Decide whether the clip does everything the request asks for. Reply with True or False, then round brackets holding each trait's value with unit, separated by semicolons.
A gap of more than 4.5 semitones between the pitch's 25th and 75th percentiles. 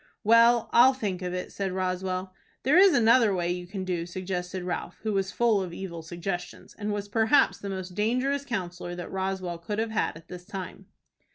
False (3.7 semitones)